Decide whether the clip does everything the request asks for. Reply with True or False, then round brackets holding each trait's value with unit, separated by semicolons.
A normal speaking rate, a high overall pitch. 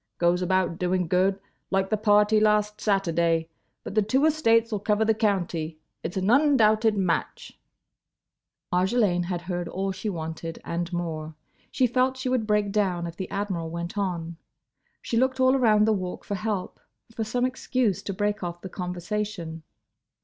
True (160 wpm; 195 Hz)